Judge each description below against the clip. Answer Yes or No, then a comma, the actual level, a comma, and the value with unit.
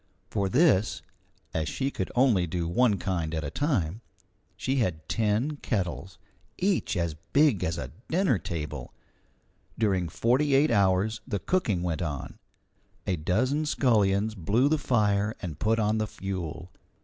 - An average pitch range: No, wide, 6.3 semitones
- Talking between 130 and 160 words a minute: Yes, average, 150 wpm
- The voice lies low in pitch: Yes, low, 100 Hz